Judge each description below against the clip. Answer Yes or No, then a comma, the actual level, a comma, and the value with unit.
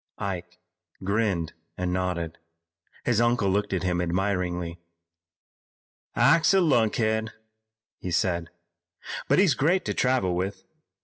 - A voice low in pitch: Yes, very low, 95 Hz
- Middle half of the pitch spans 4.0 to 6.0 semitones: Yes, average, 4.4 semitones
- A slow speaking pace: Yes, slow, 115 wpm